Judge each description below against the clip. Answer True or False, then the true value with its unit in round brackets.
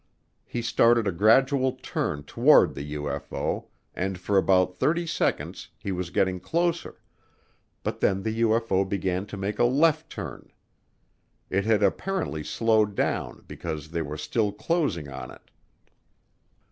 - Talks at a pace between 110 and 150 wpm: True (140 wpm)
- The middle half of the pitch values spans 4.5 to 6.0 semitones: True (4.8 semitones)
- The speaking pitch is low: True (100 Hz)